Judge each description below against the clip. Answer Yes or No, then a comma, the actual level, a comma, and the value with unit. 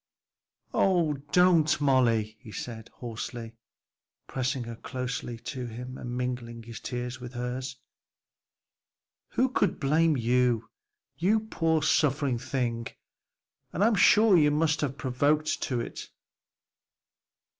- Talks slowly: Yes, slow, 120 wpm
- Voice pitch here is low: Yes, low, 130 Hz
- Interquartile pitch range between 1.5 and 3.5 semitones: No, average, 4.3 semitones